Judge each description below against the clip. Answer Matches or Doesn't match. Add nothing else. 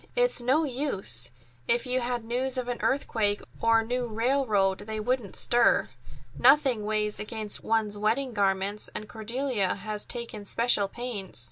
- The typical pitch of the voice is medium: Doesn't match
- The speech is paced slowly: Doesn't match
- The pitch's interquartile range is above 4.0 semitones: Doesn't match